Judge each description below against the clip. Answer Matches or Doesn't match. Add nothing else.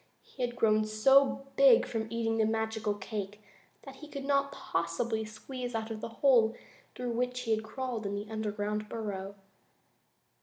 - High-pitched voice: Matches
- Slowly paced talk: Doesn't match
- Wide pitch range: Doesn't match